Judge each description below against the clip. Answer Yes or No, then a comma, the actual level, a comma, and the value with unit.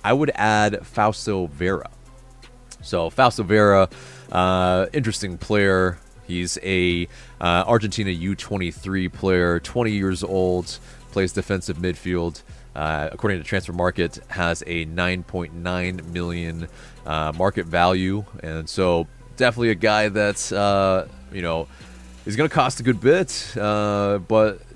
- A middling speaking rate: No, slow, 125 wpm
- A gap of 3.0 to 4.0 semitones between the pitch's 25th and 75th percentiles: Yes, average, 3.4 semitones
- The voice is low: Yes, very low, 95 Hz